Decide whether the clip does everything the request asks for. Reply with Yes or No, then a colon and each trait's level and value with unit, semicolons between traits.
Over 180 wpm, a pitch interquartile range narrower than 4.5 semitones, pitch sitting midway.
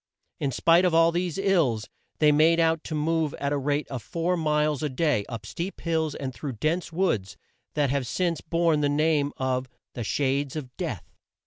Yes: average, 195 wpm; average, 3.5 semitones; medium, 150 Hz